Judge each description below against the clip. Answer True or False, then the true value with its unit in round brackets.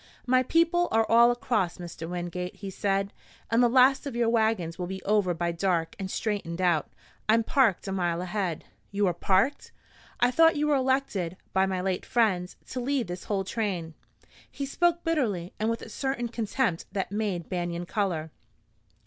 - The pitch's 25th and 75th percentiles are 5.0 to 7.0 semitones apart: True (5.3 semitones)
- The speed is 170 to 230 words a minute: True (180 wpm)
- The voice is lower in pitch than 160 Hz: False (200 Hz)